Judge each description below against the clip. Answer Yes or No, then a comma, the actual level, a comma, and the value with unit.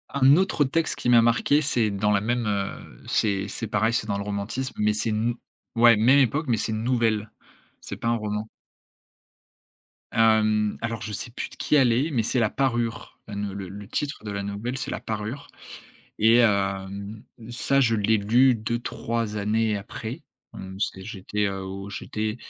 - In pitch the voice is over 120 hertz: No, low, 110 Hz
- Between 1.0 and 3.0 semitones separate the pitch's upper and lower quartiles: Yes, narrow, 2.6 semitones